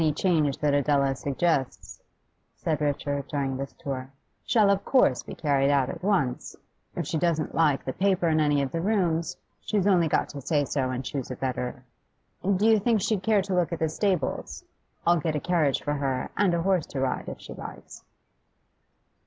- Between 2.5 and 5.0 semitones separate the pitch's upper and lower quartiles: Yes, average, 4.6 semitones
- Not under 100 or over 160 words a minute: No, average, 195 wpm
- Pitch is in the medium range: Yes, medium, 155 Hz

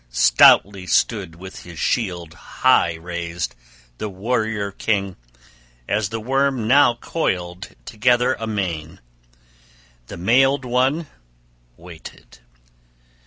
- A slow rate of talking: Yes, slow, 95 wpm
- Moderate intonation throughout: No, wide, 5.8 semitones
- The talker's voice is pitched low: Yes, low, 100 Hz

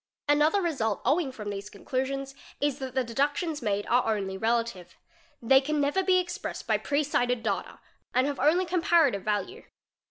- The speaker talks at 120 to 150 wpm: No, average, 170 wpm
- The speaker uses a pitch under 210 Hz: No, very high, 265 Hz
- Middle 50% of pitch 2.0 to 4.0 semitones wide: No, average, 5.3 semitones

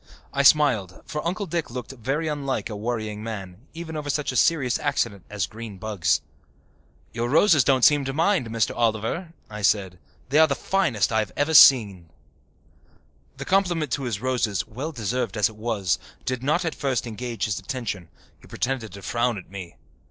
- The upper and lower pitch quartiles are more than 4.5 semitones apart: Yes, wide, 5.5 semitones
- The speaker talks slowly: No, average, 180 wpm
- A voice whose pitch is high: No, low, 120 Hz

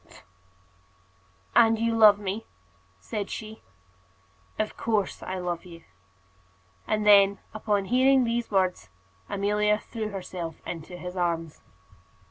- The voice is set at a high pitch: Yes, high, 205 Hz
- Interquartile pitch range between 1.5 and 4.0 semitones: Yes, average, 3.3 semitones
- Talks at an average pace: No, slow, 125 wpm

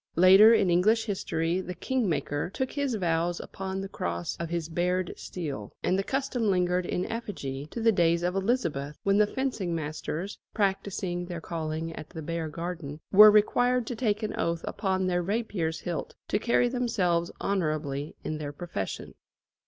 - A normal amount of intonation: Yes, average, 4.3 semitones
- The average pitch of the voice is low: No, medium, 180 Hz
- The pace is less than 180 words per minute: Yes, average, 170 wpm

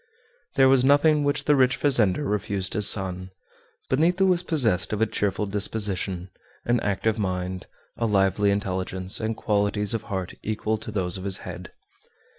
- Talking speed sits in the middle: Yes, average, 160 wpm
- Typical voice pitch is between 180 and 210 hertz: No, low, 105 Hz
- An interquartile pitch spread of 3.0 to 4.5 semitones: No, average, 5.0 semitones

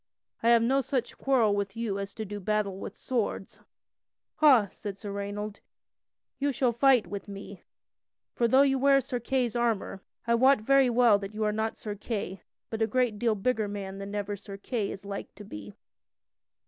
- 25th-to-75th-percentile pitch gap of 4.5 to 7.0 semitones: No, average, 3.5 semitones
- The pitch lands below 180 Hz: No, high, 215 Hz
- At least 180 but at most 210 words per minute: Yes, average, 190 wpm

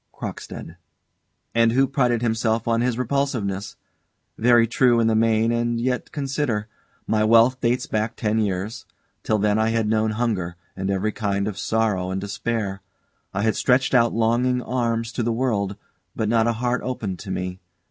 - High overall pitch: No, low, 115 Hz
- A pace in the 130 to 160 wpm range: No, average, 170 wpm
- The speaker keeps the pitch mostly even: Yes, narrow, 2.3 semitones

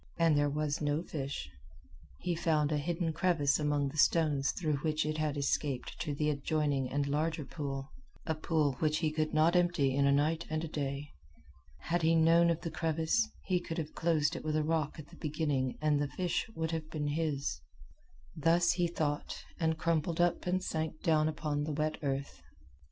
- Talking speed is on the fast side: No, average, 195 wpm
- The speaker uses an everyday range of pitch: No, narrow, 2.1 semitones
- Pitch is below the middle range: No, medium, 155 Hz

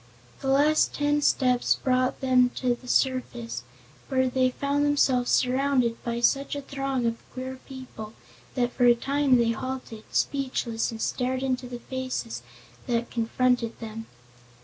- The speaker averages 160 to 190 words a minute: No, average, 150 wpm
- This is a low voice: No, very high, 255 Hz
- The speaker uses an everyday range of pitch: No, narrow, 2.1 semitones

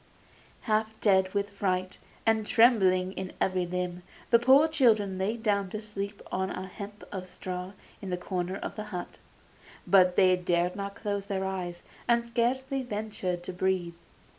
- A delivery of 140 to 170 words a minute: Yes, average, 165 wpm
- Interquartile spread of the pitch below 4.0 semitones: Yes, average, 2.9 semitones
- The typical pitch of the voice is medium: No, high, 195 Hz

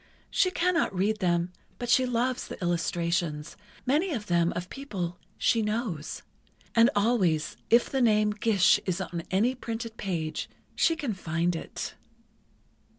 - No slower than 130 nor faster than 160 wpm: Yes, average, 140 wpm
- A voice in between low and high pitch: No, high, 205 Hz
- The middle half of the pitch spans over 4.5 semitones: Yes, wide, 5.5 semitones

